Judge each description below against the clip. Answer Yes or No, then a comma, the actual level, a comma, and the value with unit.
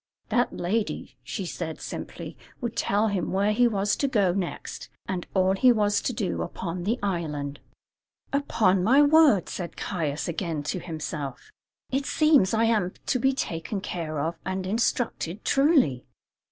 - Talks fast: No, average, 155 wpm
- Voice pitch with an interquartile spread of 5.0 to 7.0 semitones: Yes, average, 5.3 semitones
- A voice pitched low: No, high, 195 Hz